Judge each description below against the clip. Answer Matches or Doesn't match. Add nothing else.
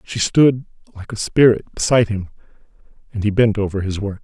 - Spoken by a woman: Doesn't match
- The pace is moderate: Matches